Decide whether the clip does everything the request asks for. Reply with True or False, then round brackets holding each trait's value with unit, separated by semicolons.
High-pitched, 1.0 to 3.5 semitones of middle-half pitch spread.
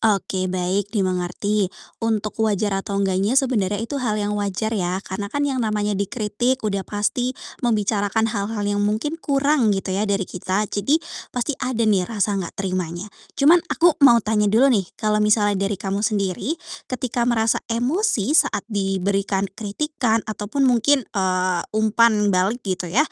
True (210 Hz; 3.2 semitones)